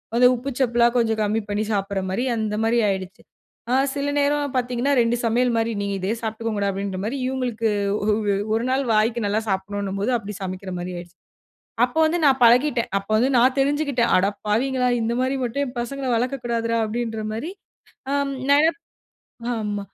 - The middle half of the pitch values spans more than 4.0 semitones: No, average, 3.7 semitones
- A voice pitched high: Yes, high, 230 Hz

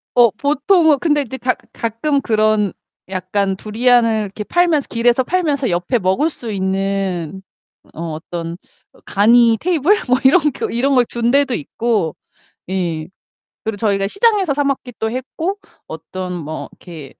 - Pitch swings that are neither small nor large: No, wide, 6.4 semitones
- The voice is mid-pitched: No, high, 230 Hz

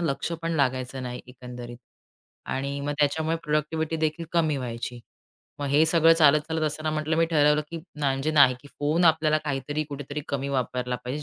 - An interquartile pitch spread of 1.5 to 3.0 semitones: Yes, average, 2.7 semitones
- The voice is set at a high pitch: No, medium, 145 Hz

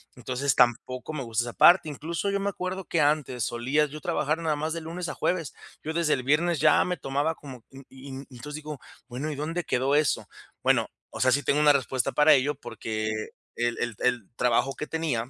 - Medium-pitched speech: Yes, medium, 145 Hz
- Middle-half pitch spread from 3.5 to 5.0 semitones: Yes, average, 4.0 semitones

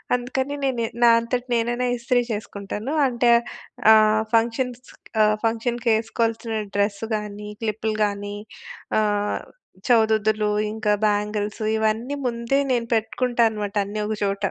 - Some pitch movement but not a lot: No, narrow, 2.2 semitones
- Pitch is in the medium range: No, high, 220 Hz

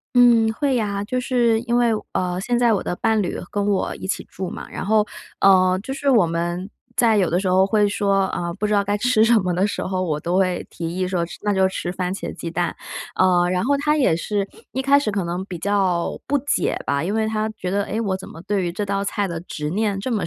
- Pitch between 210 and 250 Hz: No, high, 200 Hz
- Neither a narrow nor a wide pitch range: Yes, average, 3.4 semitones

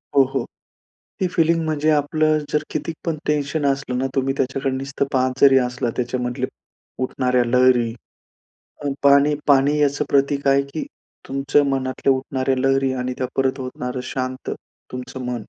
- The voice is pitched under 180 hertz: Yes, low, 135 Hz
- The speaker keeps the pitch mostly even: Yes, narrow, 2.0 semitones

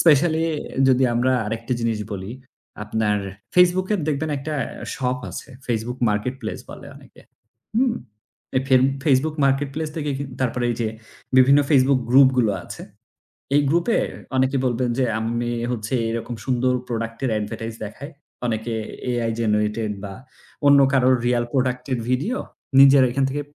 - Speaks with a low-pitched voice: Yes, low, 130 Hz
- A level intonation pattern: No, average, 3.4 semitones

